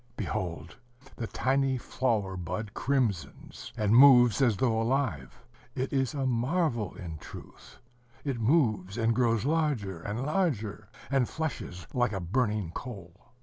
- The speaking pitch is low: Yes, low, 115 Hz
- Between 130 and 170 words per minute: Yes, slow, 135 wpm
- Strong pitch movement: No, average, 4.9 semitones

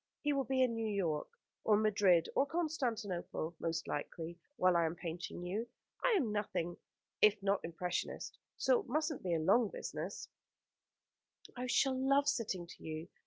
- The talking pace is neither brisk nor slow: Yes, average, 165 wpm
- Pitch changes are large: Yes, wide, 7.0 semitones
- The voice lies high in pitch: Yes, high, 205 Hz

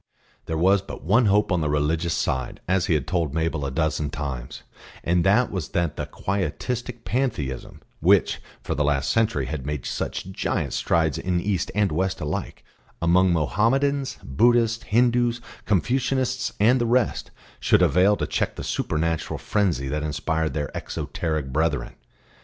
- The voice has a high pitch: No, very low, 85 Hz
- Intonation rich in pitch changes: Yes, wide, 6.6 semitones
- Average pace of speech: Yes, average, 160 wpm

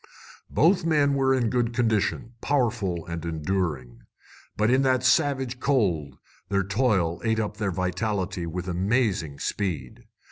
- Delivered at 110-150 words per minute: Yes, slow, 135 wpm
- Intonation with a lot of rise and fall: Yes, wide, 6.3 semitones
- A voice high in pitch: No, low, 105 Hz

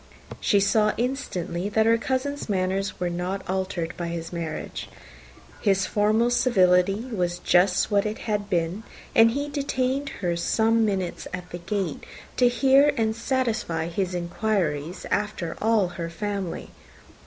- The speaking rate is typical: Yes, average, 145 wpm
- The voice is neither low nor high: No, high, 200 Hz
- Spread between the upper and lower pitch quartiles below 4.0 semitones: No, average, 4.3 semitones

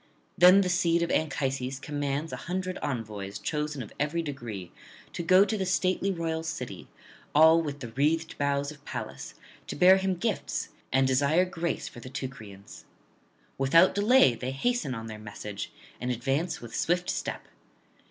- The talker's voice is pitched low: No, medium, 145 Hz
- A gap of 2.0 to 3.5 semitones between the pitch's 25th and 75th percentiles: No, average, 5.3 semitones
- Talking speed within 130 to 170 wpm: Yes, average, 160 wpm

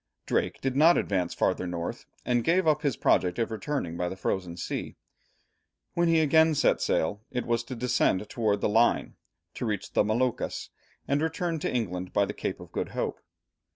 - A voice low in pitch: Yes, low, 120 Hz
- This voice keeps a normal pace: Yes, average, 190 wpm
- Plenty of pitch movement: Yes, wide, 7.4 semitones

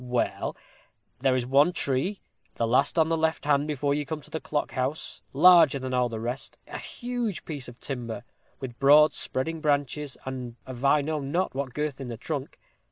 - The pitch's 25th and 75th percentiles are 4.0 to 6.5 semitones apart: No, average, 3.2 semitones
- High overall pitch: No, medium, 140 Hz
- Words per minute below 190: No, average, 195 wpm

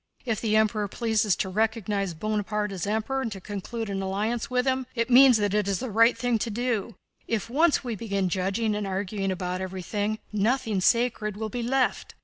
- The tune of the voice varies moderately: Yes, average, 3.0 semitones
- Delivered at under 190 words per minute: No, average, 195 wpm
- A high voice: Yes, high, 215 Hz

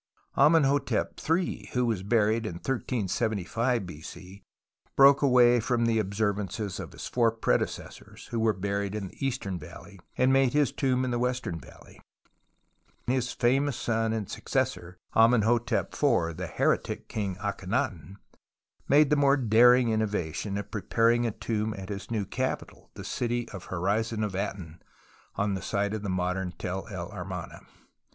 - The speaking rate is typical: Yes, average, 155 wpm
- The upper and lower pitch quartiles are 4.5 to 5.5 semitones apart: No, average, 4.1 semitones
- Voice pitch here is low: Yes, low, 110 Hz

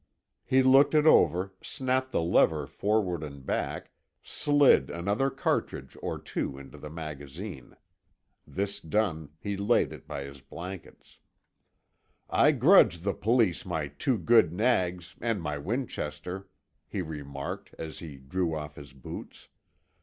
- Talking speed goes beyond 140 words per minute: No, slow, 135 wpm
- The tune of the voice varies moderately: No, wide, 6.4 semitones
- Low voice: Yes, very low, 90 Hz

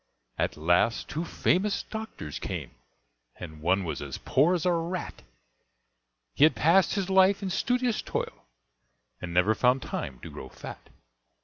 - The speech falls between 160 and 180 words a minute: No, average, 150 wpm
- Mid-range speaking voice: Yes, medium, 165 Hz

